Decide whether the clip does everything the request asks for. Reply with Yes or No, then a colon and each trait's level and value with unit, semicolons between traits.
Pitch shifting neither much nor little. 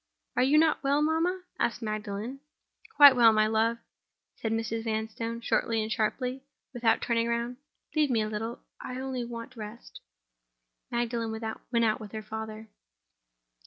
No: narrow, 2.3 semitones